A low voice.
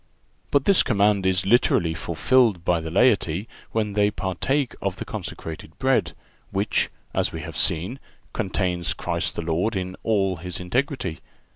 Yes: very low, 95 Hz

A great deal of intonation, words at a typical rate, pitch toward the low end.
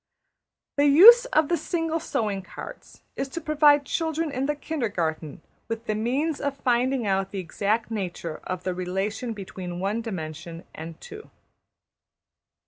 No: wide, 7.9 semitones; average, 145 wpm; high, 230 Hz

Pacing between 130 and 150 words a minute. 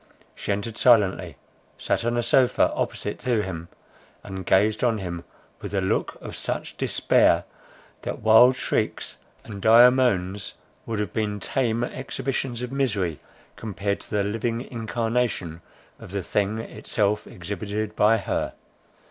Yes: average, 140 wpm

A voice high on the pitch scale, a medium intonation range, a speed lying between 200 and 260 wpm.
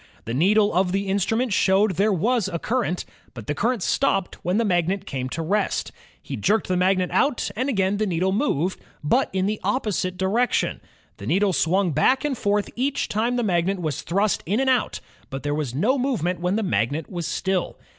Yes: high, 195 Hz; average, 3.9 semitones; fast, 205 wpm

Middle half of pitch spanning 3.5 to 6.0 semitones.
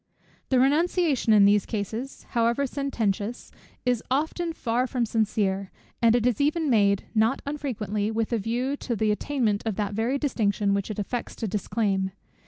Yes: average, 4.2 semitones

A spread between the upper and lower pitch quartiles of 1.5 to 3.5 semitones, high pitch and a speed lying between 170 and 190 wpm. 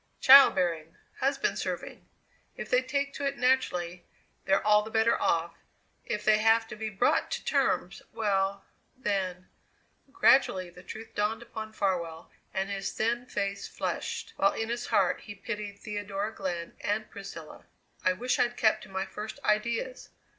No: average, 3.2 semitones; high, 210 Hz; average, 160 wpm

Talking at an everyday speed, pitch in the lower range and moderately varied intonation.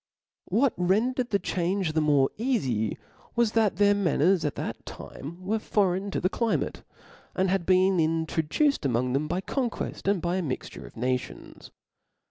No: average, 160 wpm; medium, 185 Hz; average, 4.8 semitones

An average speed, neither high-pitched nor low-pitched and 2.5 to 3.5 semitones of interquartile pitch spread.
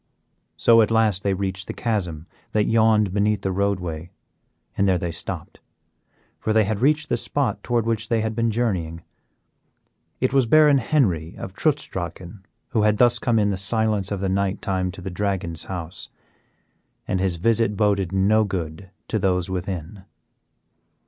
No: average, 170 wpm; low, 100 Hz; average, 3.2 semitones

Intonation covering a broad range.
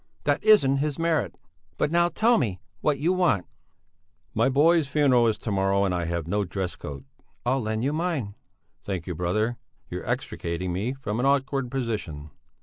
Yes: wide, 7.2 semitones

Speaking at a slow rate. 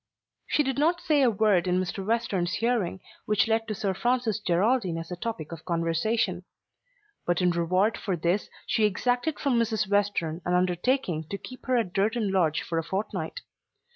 No: average, 180 wpm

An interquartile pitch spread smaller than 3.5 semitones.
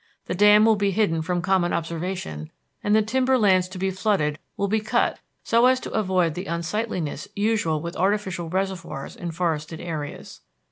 No: average, 3.8 semitones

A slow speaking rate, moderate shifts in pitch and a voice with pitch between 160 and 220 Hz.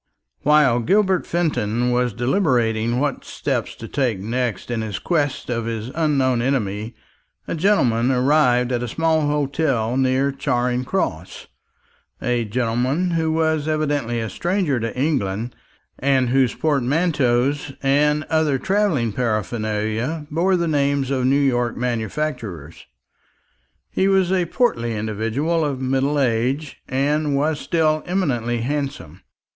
No: slow, 130 wpm; average, 4.4 semitones; low, 135 Hz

